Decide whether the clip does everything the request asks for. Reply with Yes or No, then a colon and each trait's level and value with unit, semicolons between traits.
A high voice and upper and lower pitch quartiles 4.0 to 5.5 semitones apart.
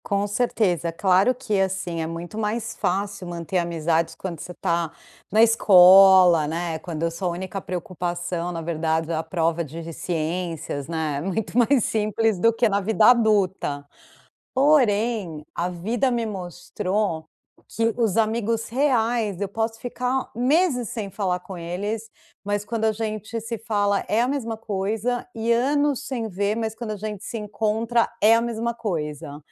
Yes: high, 205 Hz; average, 4.6 semitones